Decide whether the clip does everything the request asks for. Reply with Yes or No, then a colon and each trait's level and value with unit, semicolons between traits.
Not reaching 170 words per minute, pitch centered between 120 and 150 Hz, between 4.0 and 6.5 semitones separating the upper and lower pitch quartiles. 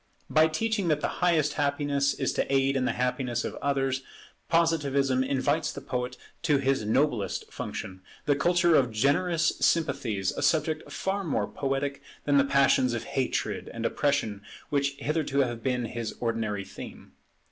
No: average, 160 wpm; medium, 140 Hz; average, 3.3 semitones